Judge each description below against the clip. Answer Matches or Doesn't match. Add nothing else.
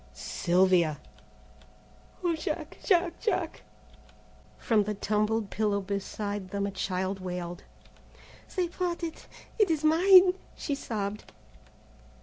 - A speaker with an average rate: Doesn't match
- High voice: Matches